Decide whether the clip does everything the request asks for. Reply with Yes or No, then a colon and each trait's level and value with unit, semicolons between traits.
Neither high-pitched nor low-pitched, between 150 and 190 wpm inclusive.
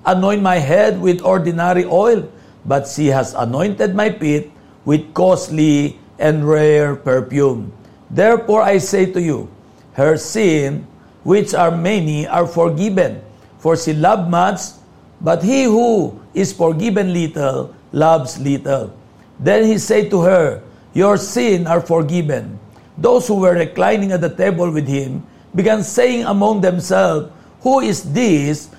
No: medium, 170 Hz; average, 140 wpm